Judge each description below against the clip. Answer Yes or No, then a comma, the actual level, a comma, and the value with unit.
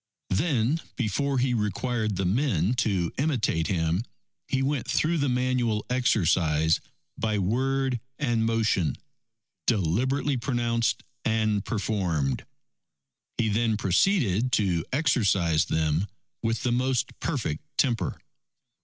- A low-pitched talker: Yes, low, 115 Hz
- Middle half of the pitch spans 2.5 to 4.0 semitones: No, average, 5.3 semitones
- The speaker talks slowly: Yes, slow, 110 wpm